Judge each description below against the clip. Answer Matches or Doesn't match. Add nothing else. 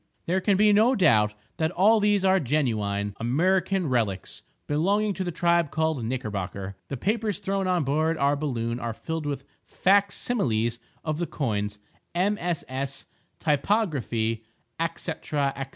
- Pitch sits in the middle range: Matches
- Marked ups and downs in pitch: Matches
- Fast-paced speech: Doesn't match